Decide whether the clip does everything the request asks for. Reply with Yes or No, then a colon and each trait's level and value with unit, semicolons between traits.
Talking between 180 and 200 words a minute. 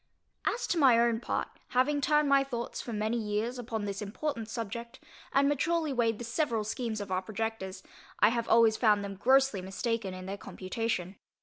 Yes: average, 185 wpm